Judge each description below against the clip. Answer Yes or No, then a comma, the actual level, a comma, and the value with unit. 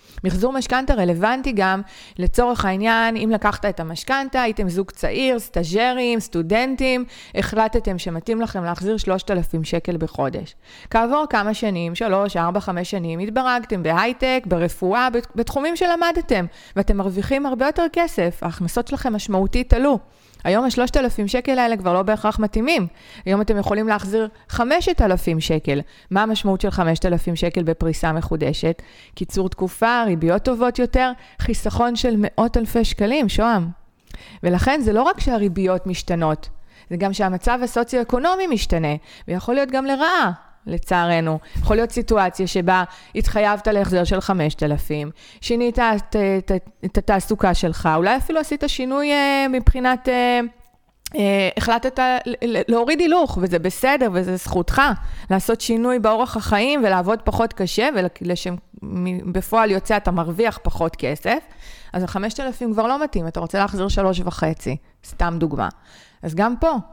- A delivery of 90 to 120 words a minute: No, average, 130 wpm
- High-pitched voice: Yes, high, 210 Hz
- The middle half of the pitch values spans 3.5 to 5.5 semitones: Yes, average, 5.1 semitones